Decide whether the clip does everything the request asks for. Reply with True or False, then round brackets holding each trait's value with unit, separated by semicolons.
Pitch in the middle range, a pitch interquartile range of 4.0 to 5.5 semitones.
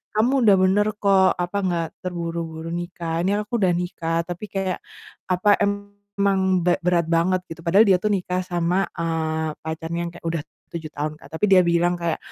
False (180 Hz; 2.7 semitones)